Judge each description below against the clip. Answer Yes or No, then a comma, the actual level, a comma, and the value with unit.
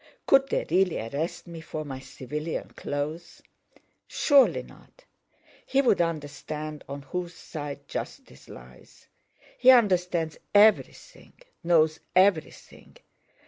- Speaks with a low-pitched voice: No, medium, 160 Hz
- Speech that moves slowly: Yes, slow, 105 wpm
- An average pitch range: Yes, average, 4.0 semitones